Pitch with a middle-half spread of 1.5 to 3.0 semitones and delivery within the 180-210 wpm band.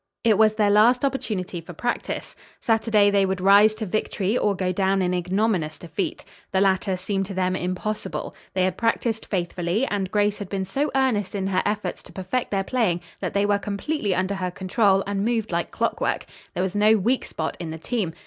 Yes: average, 2.7 semitones; average, 200 wpm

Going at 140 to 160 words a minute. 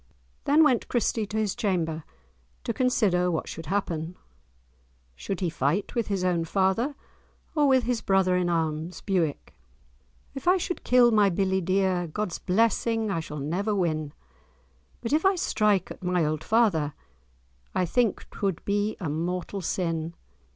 Yes: average, 155 wpm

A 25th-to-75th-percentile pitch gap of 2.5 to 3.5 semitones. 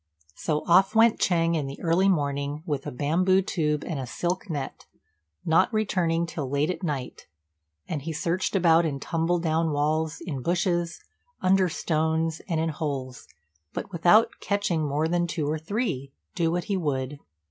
Yes: average, 3.1 semitones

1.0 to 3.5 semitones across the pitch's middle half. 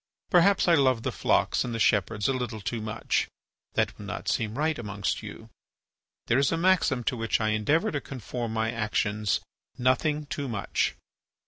No: average, 4.8 semitones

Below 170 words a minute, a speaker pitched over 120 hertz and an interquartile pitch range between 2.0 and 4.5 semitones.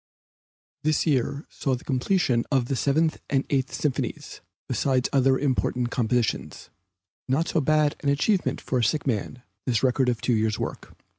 Yes: average, 160 wpm; low, 135 Hz; average, 2.8 semitones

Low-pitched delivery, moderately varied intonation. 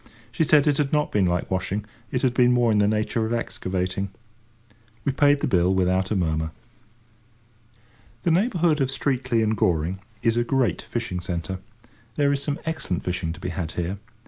No: low, 110 Hz; wide, 6.7 semitones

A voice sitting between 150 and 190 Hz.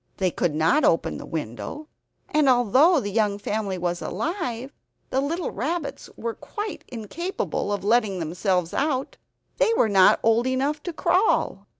No: high, 235 Hz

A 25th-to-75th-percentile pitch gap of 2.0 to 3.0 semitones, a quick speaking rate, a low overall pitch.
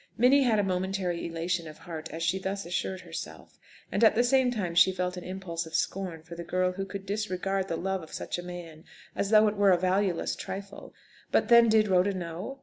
No: average, 2.7 semitones; fast, 225 wpm; medium, 185 Hz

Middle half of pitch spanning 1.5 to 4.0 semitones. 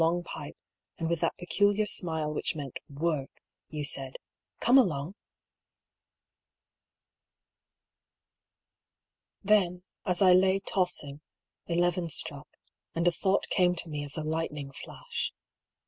Yes: average, 3.7 semitones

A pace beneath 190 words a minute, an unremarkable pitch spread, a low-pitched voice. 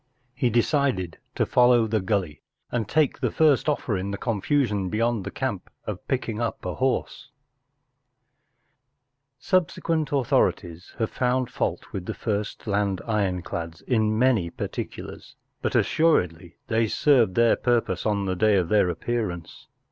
Yes: average, 155 wpm; average, 4.7 semitones; low, 110 Hz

